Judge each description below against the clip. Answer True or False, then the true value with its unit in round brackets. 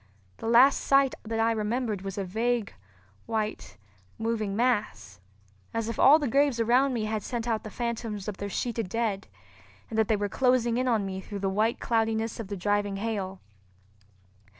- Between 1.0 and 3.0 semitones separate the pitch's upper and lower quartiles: True (2.6 semitones)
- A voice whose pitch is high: True (225 Hz)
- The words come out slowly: False (180 wpm)